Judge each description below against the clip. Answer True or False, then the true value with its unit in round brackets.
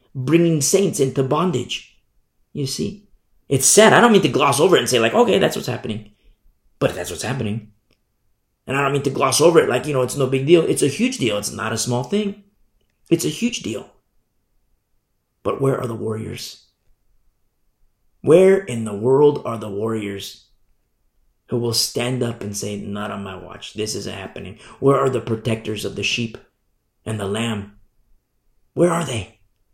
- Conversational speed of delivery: True (185 wpm)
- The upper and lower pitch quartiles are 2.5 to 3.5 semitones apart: False (4.5 semitones)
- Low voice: True (115 Hz)